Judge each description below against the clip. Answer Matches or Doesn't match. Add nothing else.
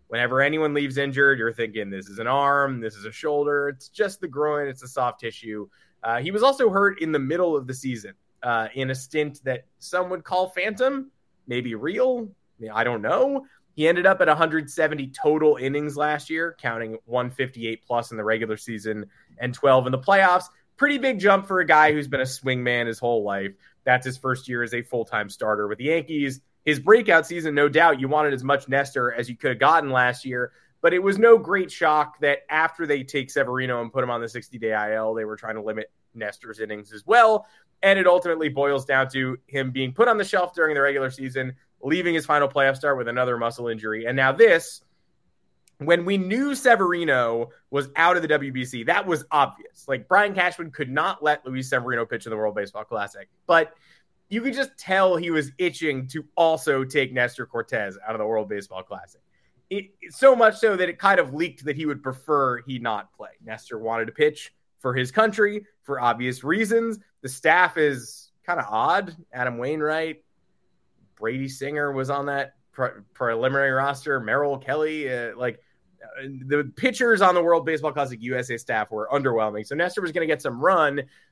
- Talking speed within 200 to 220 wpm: Matches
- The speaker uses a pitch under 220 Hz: Matches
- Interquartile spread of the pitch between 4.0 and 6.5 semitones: Matches